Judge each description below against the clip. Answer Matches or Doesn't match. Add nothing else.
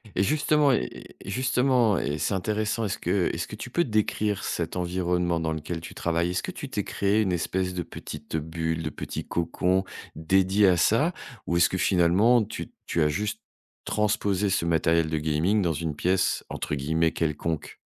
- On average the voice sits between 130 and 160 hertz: Doesn't match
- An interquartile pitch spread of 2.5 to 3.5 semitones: Doesn't match